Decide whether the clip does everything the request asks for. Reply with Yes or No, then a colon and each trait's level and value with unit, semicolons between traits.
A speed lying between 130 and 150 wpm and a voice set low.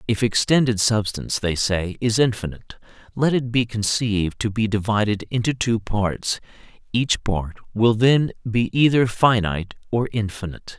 Yes: average, 145 wpm; low, 110 Hz